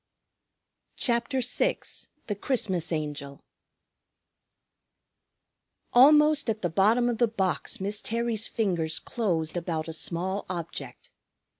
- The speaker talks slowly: Yes, slow, 105 wpm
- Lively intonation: Yes, wide, 6.0 semitones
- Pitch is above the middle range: Yes, high, 200 Hz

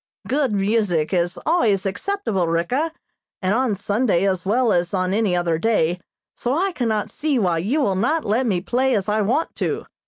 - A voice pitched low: No, high, 210 Hz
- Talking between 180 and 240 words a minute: Yes, average, 185 wpm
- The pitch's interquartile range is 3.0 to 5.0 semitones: No, wide, 5.6 semitones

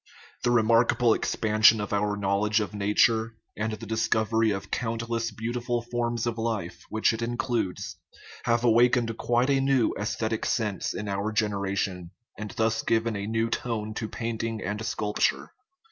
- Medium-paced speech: Yes, average, 160 wpm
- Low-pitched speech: Yes, low, 110 Hz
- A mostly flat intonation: Yes, narrow, 1.8 semitones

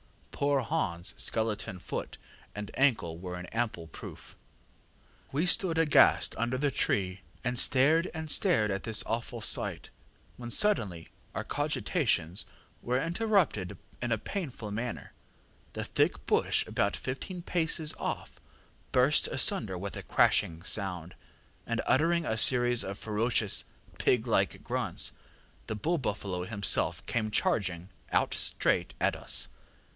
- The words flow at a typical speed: No, slow, 130 wpm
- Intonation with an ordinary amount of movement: No, wide, 6.4 semitones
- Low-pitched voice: Yes, low, 115 Hz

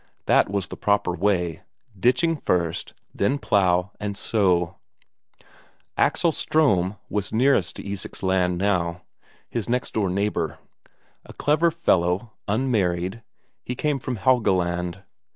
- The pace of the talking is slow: Yes, slow, 120 wpm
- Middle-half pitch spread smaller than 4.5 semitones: No, average, 5.2 semitones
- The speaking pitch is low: Yes, low, 100 Hz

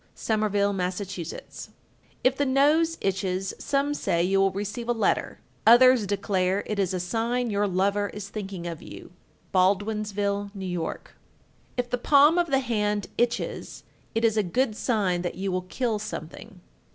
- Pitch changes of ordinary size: Yes, average, 3.9 semitones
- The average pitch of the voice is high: Yes, high, 205 Hz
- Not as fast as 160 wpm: No, average, 165 wpm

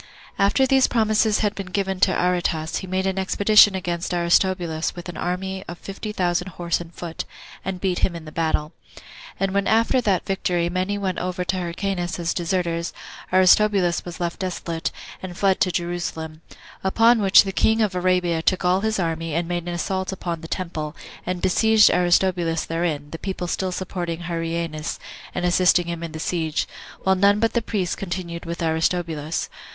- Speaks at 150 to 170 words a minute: No, average, 180 wpm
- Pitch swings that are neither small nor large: No, narrow, 2.1 semitones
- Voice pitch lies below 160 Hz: No, medium, 180 Hz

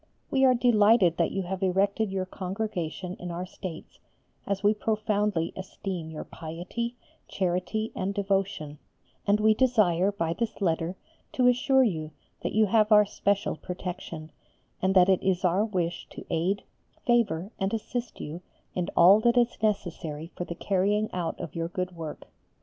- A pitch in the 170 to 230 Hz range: Yes, high, 190 Hz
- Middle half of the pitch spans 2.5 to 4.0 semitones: Yes, average, 3.5 semitones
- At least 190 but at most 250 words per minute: No, average, 160 wpm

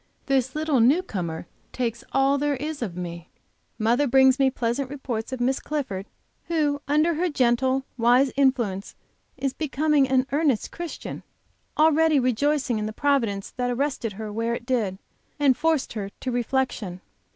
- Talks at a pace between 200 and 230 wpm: No, average, 155 wpm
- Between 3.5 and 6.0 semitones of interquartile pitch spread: Yes, average, 3.8 semitones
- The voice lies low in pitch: No, very high, 260 Hz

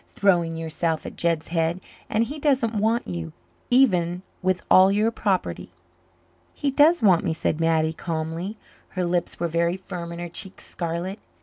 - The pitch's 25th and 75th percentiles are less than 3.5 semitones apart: No, average, 4.0 semitones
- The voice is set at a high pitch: No, medium, 175 Hz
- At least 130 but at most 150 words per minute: No, average, 165 wpm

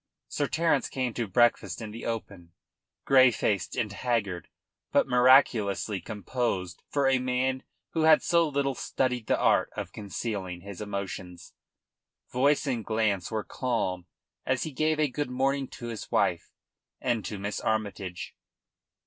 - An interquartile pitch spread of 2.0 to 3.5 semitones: No, average, 4.6 semitones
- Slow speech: No, average, 150 wpm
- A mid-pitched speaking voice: No, low, 120 Hz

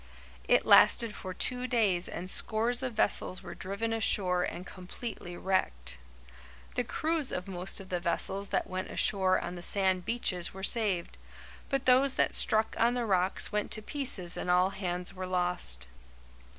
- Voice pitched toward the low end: No, high, 190 Hz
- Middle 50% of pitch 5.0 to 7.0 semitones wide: No, average, 4.1 semitones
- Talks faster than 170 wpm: No, average, 165 wpm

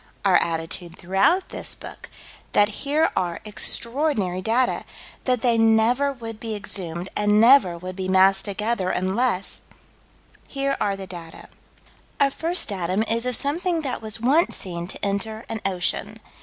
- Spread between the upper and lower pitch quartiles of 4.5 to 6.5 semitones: Yes, average, 5.0 semitones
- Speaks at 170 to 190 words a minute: No, average, 150 wpm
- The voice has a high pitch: Yes, high, 215 Hz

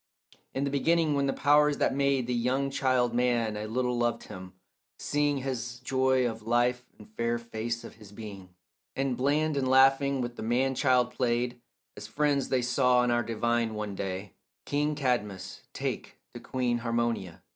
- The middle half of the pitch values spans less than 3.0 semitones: Yes, narrow, 2.5 semitones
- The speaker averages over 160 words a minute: Yes, average, 175 wpm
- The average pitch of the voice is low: Yes, low, 125 Hz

